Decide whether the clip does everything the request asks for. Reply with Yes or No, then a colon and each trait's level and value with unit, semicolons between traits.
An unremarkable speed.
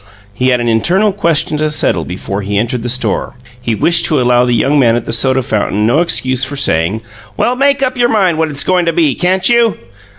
No: fast, 230 wpm